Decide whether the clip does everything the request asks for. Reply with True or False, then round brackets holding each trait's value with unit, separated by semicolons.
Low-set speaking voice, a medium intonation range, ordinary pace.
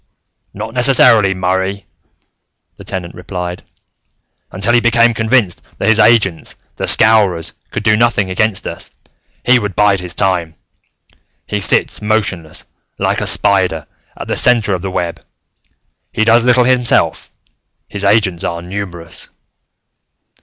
False (100 Hz; 3.6 semitones; 130 wpm)